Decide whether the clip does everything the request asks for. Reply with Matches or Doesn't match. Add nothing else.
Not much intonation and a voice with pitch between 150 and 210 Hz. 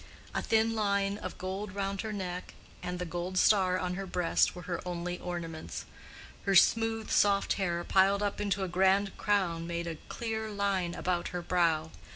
Matches